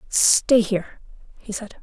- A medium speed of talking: No, slow, 130 wpm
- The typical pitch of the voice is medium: No, high, 210 Hz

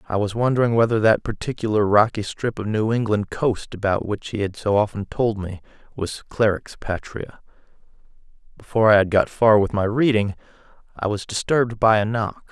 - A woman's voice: No, male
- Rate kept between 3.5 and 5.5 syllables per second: Yes, 5.3 syllables/s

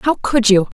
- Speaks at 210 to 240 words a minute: Yes, fast, 230 wpm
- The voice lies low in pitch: No, high, 230 Hz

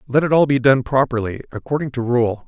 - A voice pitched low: Yes, low, 125 Hz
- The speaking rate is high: Yes, fast, 220 wpm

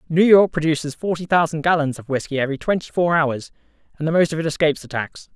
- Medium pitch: Yes, medium, 155 Hz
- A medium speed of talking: No, fast, 225 wpm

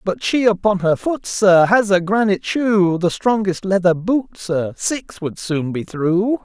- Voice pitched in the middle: No, high, 195 Hz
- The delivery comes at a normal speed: Yes, average, 185 wpm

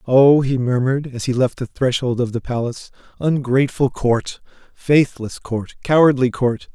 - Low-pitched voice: Yes, low, 130 Hz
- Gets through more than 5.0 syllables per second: No, 4.7 syllables/s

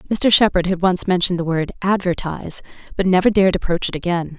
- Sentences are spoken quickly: No, average, 190 wpm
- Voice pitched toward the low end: No, medium, 180 Hz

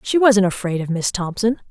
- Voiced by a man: No, female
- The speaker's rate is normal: No, fast, 210 wpm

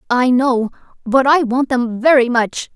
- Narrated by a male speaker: No, female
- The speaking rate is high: No, average, 175 wpm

